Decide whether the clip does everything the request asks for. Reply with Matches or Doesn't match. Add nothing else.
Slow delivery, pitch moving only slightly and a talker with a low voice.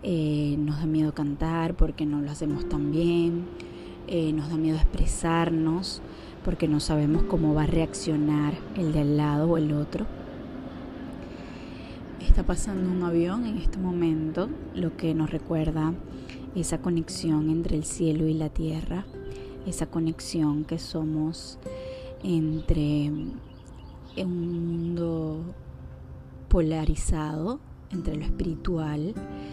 Doesn't match